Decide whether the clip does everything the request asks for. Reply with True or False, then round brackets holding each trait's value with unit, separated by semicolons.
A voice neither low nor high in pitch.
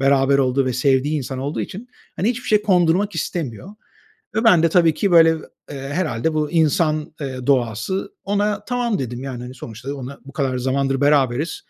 True (145 Hz)